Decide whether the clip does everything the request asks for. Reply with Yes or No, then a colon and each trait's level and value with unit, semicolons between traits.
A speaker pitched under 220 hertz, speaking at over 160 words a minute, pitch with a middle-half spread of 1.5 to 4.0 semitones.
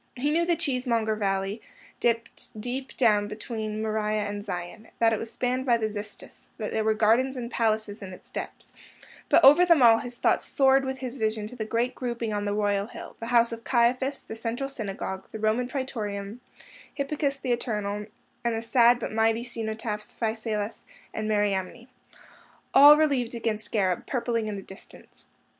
No: high, 225 Hz; average, 175 wpm; average, 2.8 semitones